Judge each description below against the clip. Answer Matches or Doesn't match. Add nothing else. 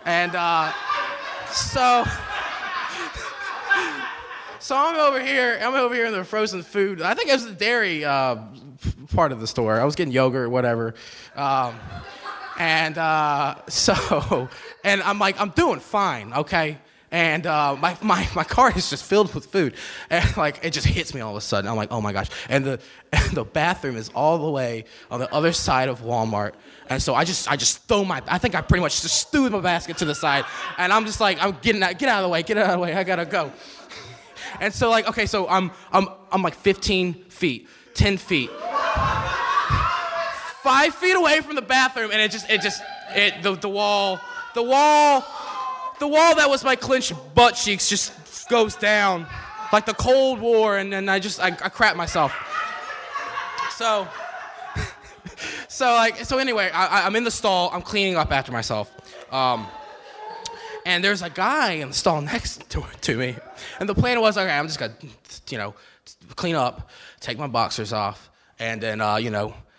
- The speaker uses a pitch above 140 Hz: Matches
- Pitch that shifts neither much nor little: Doesn't match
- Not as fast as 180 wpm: Doesn't match